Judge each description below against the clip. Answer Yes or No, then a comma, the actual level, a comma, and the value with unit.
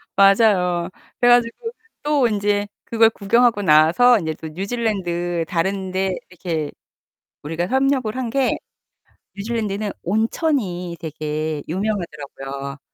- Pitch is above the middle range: Yes, high, 195 Hz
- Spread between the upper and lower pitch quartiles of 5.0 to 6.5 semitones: Yes, wide, 5.4 semitones